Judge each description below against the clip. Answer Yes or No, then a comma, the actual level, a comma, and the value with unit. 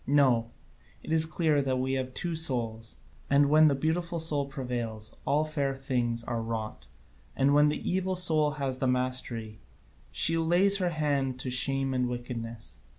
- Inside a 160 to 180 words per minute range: Yes, average, 165 wpm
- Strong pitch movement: No, average, 4.0 semitones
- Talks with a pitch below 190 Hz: Yes, low, 135 Hz